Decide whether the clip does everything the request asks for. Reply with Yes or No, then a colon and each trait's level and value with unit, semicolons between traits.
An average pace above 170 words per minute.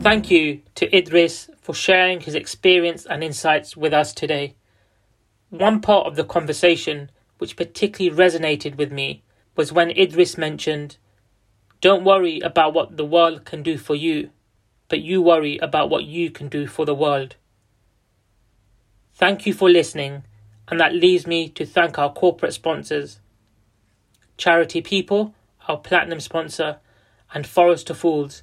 No: average, 145 wpm